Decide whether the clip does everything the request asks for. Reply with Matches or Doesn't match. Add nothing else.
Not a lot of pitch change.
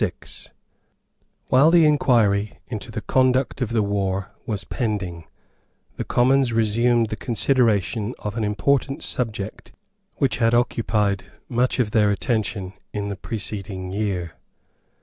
Doesn't match